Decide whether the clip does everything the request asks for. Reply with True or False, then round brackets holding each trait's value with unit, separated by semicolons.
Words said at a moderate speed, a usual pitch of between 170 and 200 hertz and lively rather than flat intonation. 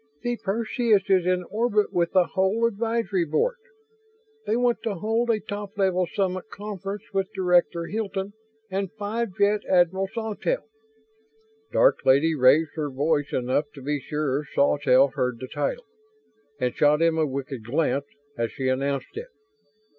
True (150 wpm; 185 Hz; 6.4 semitones)